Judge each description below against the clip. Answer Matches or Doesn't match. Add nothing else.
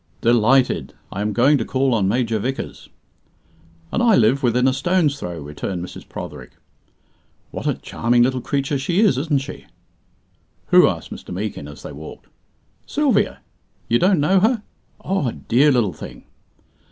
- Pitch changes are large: Doesn't match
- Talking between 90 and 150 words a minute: Doesn't match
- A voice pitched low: Matches